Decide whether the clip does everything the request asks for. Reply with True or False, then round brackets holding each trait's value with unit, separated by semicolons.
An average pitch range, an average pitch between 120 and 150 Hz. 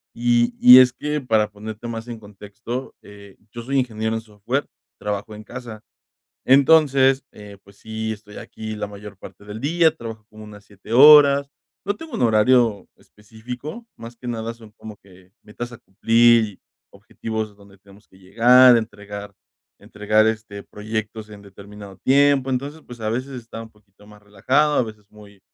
False (3.1 semitones; 110 Hz)